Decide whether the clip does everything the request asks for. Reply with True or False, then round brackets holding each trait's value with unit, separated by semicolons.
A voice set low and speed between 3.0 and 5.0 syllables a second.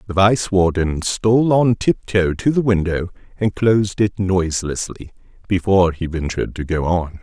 True (95 Hz; 4.9 syllables/s)